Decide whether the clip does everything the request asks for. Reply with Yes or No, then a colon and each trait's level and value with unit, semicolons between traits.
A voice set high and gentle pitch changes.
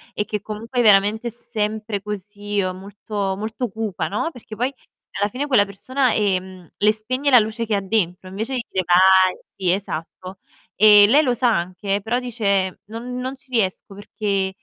No: high, 210 Hz; average, 3.1 semitones